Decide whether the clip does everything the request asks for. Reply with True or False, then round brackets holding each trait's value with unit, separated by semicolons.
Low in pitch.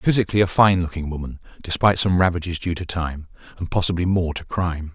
True (85 Hz)